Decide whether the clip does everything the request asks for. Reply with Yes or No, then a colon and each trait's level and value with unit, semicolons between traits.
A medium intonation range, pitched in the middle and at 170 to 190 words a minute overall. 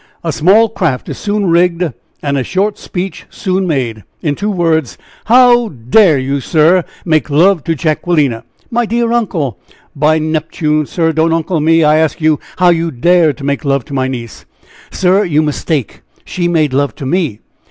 Yes: average, 4.2 semitones; medium, 160 Hz; average, 180 wpm